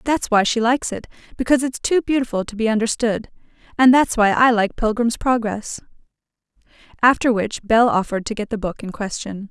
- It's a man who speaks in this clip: No, female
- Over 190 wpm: No, average, 175 wpm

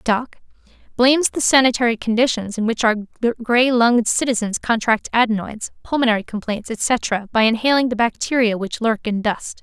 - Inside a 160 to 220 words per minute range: No, average, 145 wpm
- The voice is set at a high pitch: Yes, high, 230 Hz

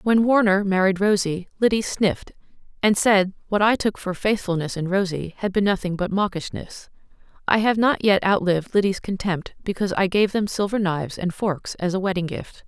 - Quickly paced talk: No, average, 185 wpm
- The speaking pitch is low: No, high, 195 Hz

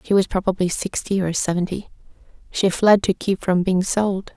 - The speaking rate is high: No, average, 180 wpm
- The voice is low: No, high, 190 Hz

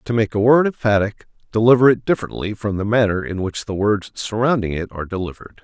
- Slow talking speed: No, average, 200 wpm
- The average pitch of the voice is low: Yes, low, 105 Hz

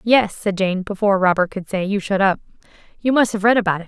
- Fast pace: Yes, fast, 250 wpm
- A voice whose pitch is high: Yes, high, 200 Hz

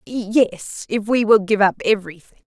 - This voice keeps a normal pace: Yes, average, 170 wpm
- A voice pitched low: No, high, 210 Hz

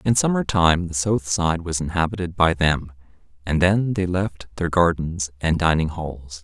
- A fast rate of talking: No, average, 175 wpm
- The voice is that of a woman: No, male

